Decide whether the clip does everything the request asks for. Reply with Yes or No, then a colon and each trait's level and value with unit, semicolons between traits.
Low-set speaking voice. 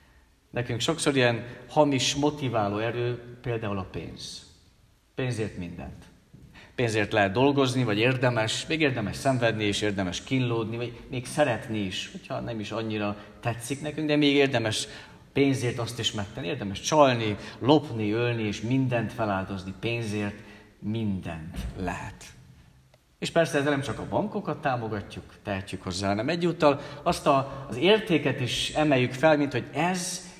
Yes: low, 120 Hz